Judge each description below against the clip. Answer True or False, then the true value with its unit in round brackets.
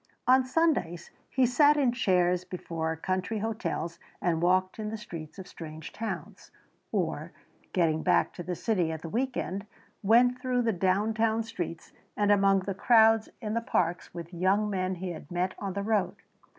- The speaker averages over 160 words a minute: True (175 wpm)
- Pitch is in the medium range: False (195 Hz)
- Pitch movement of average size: True (4.2 semitones)